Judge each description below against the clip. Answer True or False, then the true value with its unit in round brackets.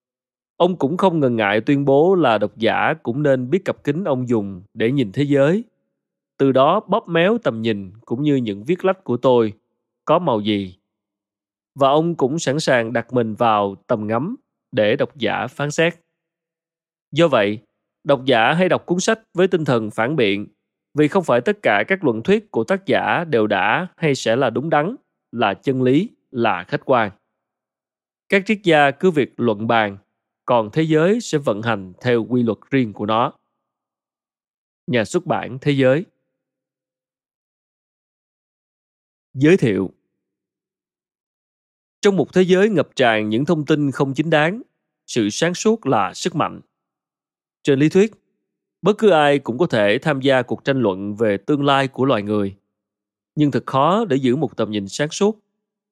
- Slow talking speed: False (175 wpm)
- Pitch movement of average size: False (6.7 semitones)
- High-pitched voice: False (135 Hz)